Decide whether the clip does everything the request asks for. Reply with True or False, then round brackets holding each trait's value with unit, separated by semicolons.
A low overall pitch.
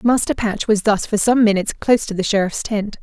False (210 Hz)